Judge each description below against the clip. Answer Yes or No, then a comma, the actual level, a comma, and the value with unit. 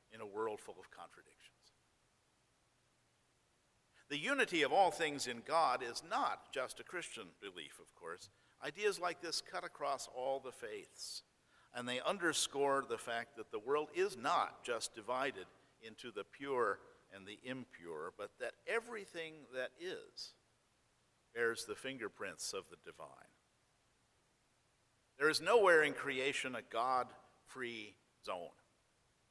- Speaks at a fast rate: No, slow, 135 wpm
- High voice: No, low, 135 Hz